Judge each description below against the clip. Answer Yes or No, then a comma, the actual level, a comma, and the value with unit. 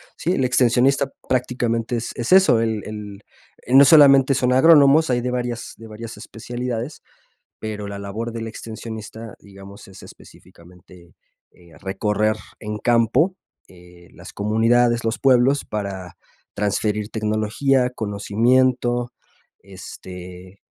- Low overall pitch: Yes, low, 115 Hz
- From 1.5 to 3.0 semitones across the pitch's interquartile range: No, average, 3.4 semitones